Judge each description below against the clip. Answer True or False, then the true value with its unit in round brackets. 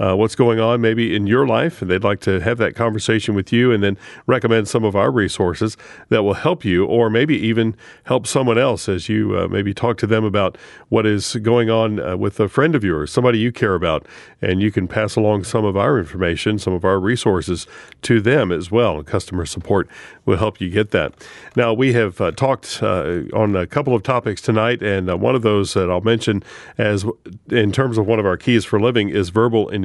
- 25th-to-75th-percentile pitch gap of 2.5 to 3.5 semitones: True (2.8 semitones)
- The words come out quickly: True (230 wpm)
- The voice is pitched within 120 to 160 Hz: False (110 Hz)